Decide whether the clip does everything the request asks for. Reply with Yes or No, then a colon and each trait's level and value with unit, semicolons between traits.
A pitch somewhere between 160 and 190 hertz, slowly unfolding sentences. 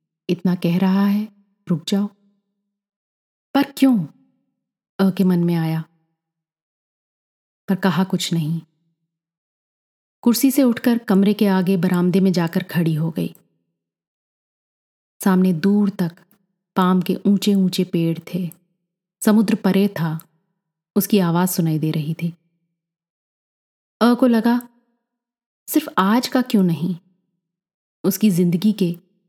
No: medium, 185 Hz; average, 120 wpm